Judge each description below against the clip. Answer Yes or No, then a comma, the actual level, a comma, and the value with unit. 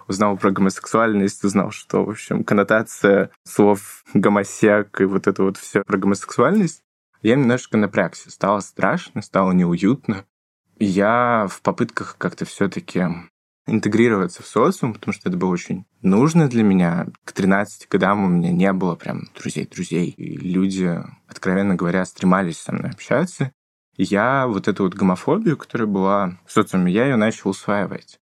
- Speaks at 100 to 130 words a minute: No, average, 150 wpm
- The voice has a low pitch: Yes, low, 100 Hz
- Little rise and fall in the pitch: Yes, narrow, 2.0 semitones